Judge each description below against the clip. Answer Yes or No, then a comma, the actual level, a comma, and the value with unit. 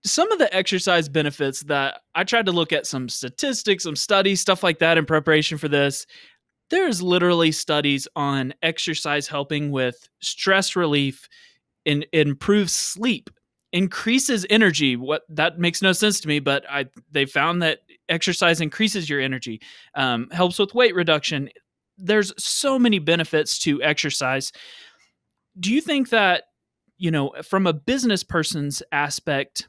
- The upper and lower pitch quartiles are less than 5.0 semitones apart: No, wide, 5.4 semitones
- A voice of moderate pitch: Yes, medium, 165 Hz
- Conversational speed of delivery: Yes, average, 150 wpm